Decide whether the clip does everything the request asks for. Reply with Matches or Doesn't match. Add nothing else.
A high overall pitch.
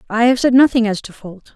Matches